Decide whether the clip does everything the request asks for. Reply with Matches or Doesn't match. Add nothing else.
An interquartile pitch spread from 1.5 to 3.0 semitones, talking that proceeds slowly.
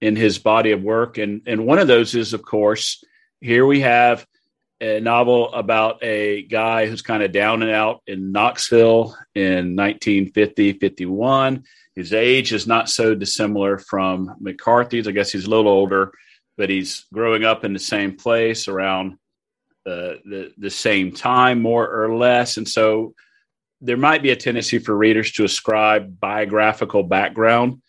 Doesn't match